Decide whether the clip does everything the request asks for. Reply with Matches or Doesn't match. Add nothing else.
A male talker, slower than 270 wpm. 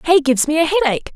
Doesn't match